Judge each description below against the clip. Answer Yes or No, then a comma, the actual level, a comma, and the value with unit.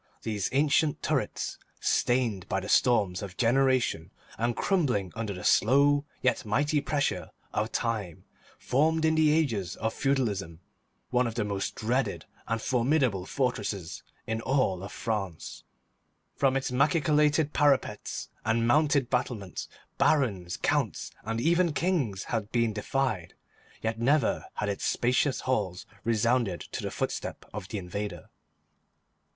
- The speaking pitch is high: No, low, 115 Hz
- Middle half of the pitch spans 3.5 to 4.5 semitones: No, wide, 5.4 semitones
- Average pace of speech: No, slow, 130 wpm